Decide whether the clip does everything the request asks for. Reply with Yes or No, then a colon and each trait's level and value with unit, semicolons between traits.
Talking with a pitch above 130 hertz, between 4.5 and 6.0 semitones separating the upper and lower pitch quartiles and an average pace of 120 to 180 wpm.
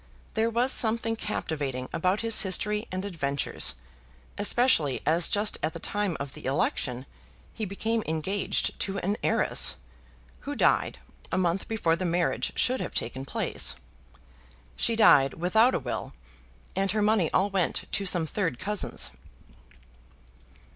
Yes: high, 190 Hz; average, 4.9 semitones; average, 140 wpm